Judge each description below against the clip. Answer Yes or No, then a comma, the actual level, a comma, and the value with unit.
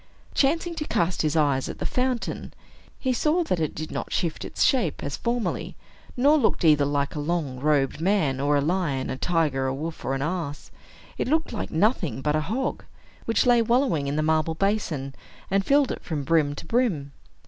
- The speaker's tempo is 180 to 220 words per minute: Yes, average, 200 wpm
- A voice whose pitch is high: No, medium, 165 Hz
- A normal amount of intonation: No, wide, 8.3 semitones